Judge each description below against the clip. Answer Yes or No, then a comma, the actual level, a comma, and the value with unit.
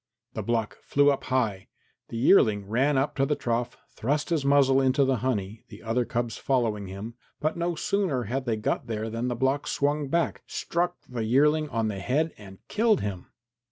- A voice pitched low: Yes, low, 130 Hz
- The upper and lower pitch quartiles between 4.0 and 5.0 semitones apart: Yes, average, 4.4 semitones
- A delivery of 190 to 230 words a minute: Yes, average, 195 wpm